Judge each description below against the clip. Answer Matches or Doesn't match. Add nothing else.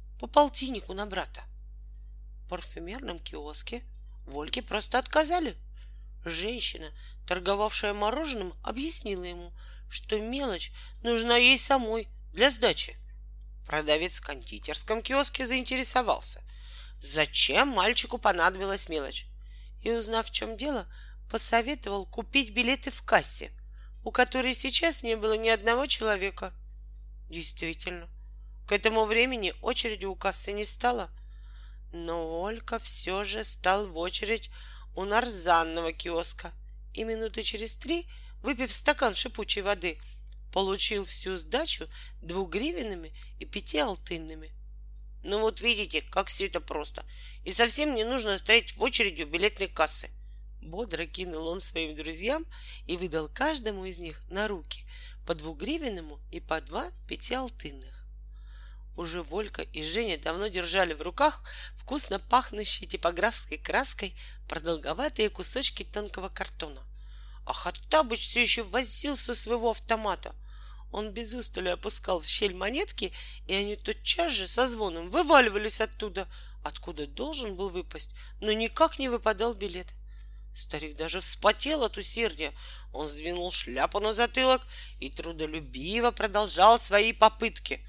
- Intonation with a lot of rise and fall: Matches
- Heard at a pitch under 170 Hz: Doesn't match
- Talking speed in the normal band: Matches